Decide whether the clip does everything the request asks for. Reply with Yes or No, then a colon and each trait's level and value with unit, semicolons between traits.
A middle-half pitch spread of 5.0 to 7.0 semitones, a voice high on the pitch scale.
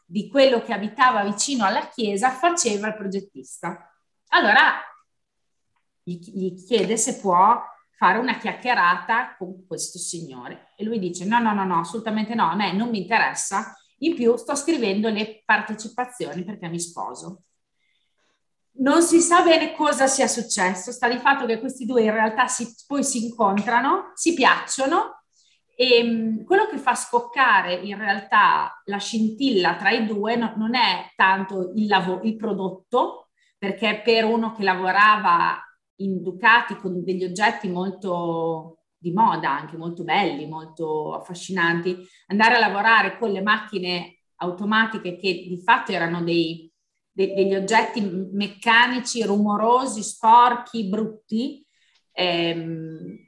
No: average, 4.5 semitones; high, 215 Hz